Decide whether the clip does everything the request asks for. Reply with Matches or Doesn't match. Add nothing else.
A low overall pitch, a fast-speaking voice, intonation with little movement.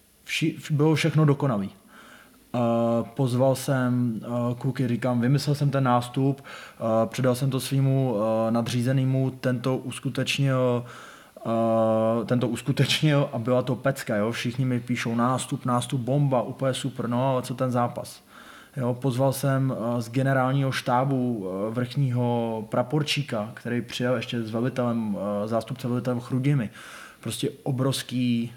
Doesn't match